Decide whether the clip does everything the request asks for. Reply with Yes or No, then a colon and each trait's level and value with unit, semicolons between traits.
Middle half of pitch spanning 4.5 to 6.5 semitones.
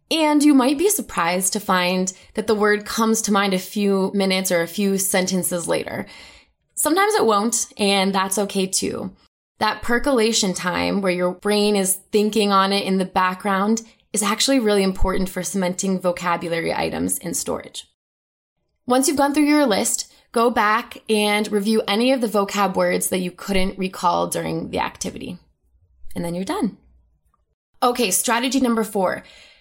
No: average, 3.5 semitones